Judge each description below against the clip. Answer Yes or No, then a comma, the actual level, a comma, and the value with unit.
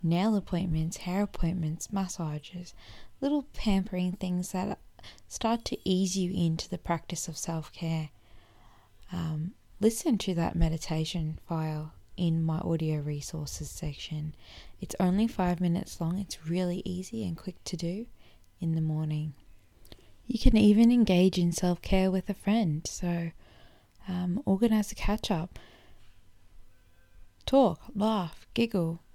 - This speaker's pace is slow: Yes, slow, 130 wpm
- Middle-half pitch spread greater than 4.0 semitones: No, average, 3.5 semitones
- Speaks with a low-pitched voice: No, medium, 175 Hz